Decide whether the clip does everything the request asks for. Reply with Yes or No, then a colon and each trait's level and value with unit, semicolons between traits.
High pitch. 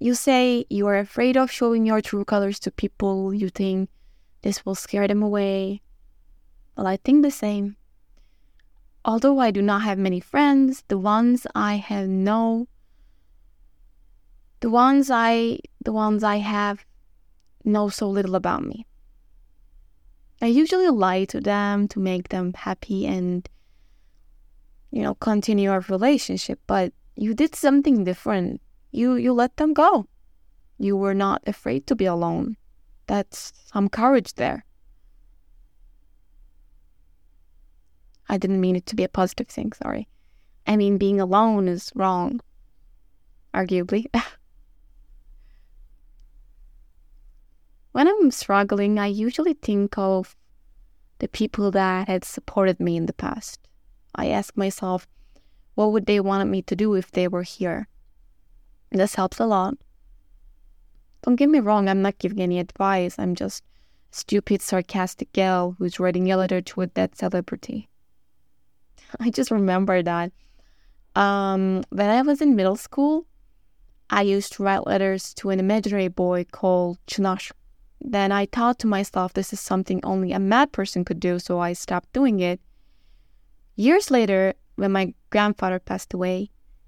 Yes: high, 195 Hz